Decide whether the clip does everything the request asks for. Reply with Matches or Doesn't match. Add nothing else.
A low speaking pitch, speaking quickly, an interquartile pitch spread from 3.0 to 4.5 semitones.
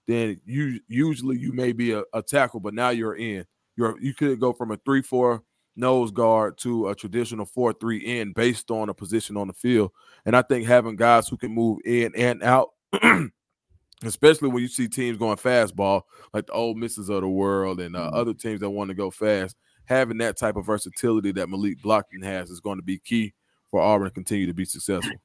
Matches